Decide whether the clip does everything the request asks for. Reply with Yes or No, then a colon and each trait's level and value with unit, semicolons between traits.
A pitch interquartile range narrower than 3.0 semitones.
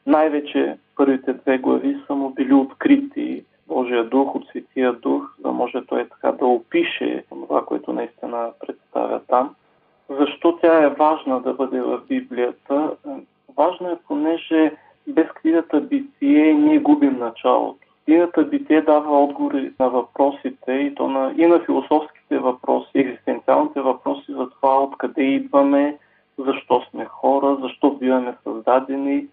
No: average, 3.7 semitones